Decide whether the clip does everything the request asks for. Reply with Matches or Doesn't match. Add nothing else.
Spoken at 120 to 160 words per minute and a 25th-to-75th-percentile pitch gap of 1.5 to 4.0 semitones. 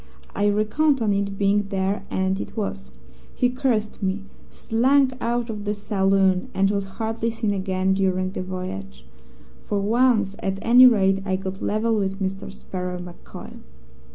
Matches